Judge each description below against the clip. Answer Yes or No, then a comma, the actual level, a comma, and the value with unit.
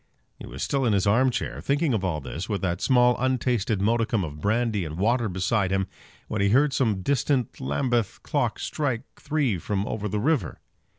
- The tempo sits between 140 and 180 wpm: No, average, 190 wpm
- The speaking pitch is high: No, low, 110 Hz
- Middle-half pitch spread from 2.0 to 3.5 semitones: No, average, 4.8 semitones